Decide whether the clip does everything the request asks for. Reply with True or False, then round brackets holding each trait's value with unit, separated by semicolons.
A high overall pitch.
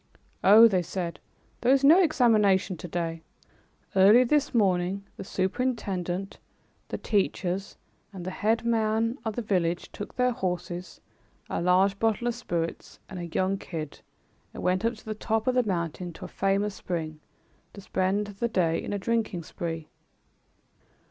True (195 Hz)